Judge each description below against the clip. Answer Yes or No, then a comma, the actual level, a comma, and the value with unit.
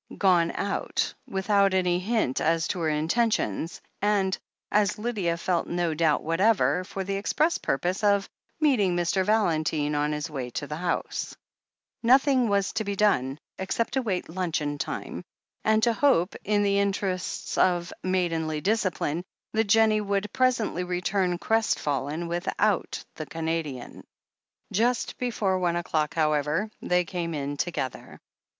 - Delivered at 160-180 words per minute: No, average, 145 wpm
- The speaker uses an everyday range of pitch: Yes, average, 4.2 semitones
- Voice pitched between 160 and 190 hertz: Yes, medium, 185 Hz